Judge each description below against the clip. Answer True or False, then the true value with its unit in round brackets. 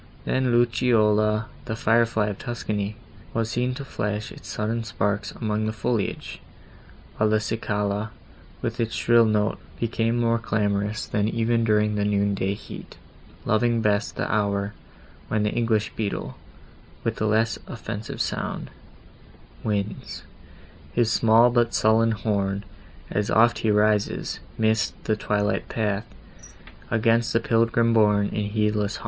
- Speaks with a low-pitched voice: True (110 Hz)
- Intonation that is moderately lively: False (1.8 semitones)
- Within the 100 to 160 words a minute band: True (140 wpm)